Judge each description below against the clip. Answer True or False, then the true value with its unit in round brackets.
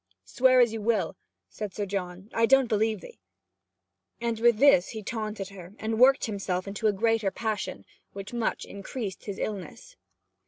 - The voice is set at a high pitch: True (215 Hz)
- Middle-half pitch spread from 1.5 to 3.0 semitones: True (2.7 semitones)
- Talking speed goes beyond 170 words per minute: False (165 wpm)